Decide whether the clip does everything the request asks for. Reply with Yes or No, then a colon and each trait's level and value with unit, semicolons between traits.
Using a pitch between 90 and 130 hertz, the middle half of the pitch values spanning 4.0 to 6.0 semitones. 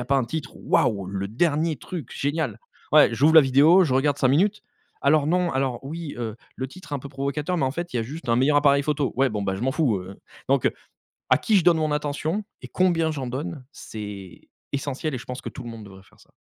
No: medium, 140 Hz; average, 4.3 semitones